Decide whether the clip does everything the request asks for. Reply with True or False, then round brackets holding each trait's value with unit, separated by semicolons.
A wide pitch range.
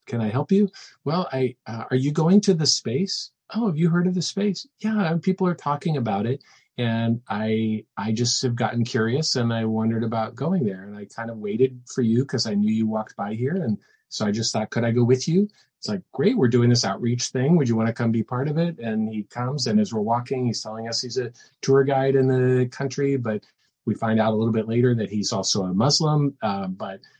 False (4.5 semitones)